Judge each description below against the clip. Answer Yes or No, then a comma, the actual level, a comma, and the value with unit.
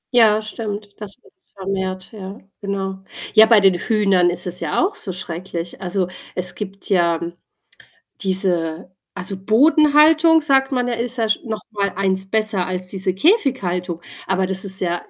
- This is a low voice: No, high, 195 Hz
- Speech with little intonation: No, average, 3.2 semitones